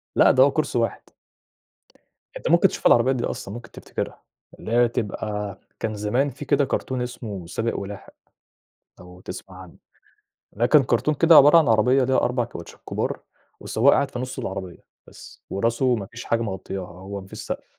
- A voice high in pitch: No, low, 115 Hz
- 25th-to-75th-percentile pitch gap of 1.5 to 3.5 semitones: No, average, 4.4 semitones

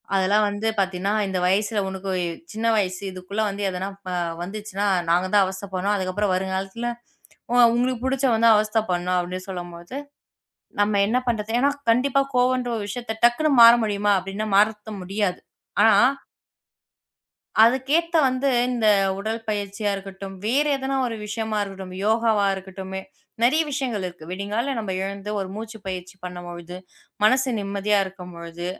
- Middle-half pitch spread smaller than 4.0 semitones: Yes, average, 3.3 semitones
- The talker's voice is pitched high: Yes, high, 205 Hz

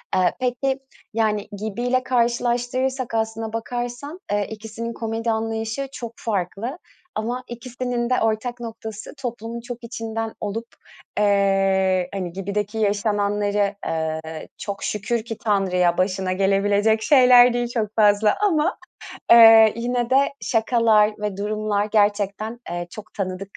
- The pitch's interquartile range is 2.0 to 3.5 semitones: Yes, average, 2.8 semitones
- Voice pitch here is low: No, high, 220 Hz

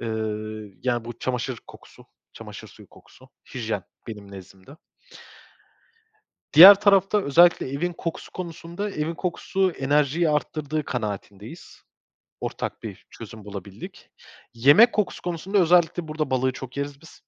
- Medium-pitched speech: Yes, medium, 150 Hz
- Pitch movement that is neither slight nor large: No, wide, 6.0 semitones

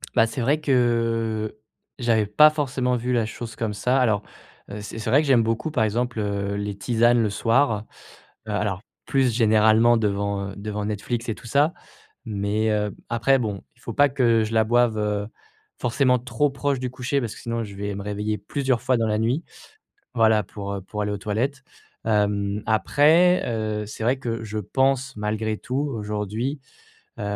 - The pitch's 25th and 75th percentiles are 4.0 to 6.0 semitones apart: No, average, 3.1 semitones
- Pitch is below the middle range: Yes, low, 115 Hz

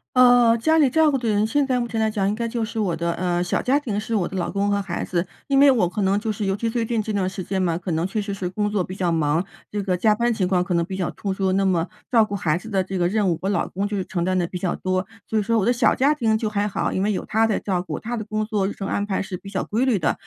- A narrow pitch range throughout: No, average, 3.3 semitones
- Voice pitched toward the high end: Yes, high, 205 Hz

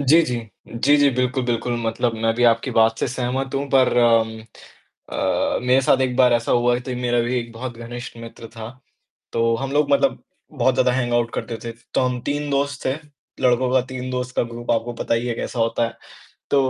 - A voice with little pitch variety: Yes, narrow, 1.9 semitones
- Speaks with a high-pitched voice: No, low, 120 Hz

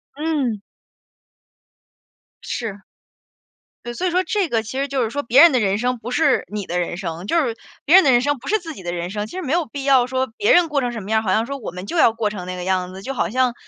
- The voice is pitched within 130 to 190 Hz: No, high, 240 Hz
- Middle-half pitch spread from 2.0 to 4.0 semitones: No, wide, 5.5 semitones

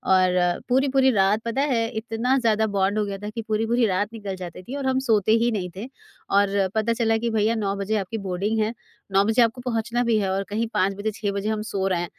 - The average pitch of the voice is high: Yes, high, 215 Hz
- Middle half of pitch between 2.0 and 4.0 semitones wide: Yes, average, 2.7 semitones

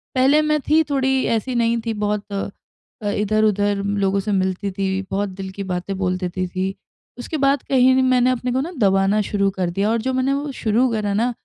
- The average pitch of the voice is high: Yes, high, 210 Hz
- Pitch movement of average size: Yes, average, 4.7 semitones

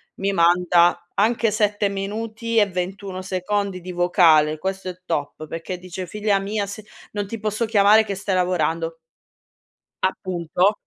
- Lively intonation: No, average, 2.7 semitones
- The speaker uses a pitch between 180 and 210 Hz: Yes, high, 190 Hz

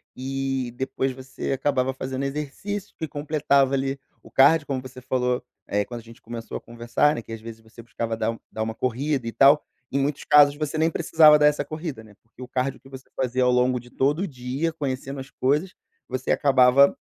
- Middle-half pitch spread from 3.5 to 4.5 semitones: No, average, 2.7 semitones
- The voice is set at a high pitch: No, low, 135 Hz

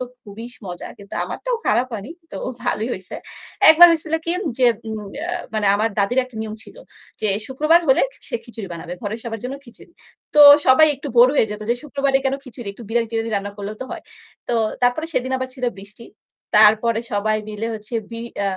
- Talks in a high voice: Yes, high, 230 Hz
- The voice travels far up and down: No, average, 3.7 semitones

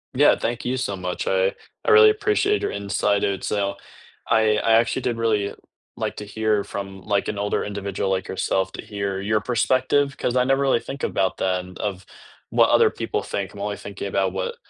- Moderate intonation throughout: Yes, average, 3.8 semitones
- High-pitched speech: No, low, 105 Hz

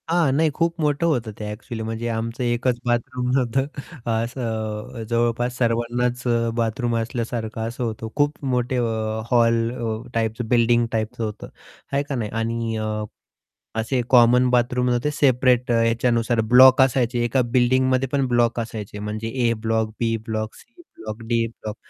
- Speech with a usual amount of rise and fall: No, narrow, 1.9 semitones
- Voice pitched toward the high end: No, low, 120 Hz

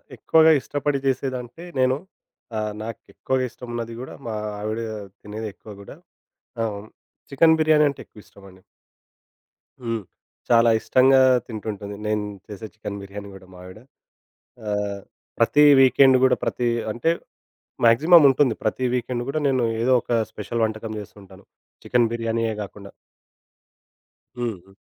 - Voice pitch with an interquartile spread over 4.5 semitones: No, average, 3.7 semitones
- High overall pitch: No, low, 115 Hz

